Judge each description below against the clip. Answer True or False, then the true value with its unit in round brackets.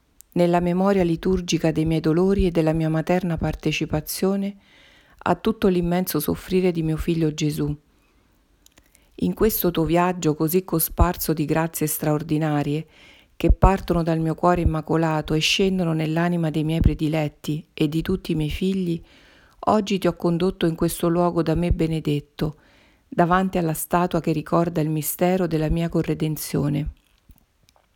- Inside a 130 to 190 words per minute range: True (140 wpm)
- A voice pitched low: False (165 Hz)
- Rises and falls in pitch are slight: True (2.3 semitones)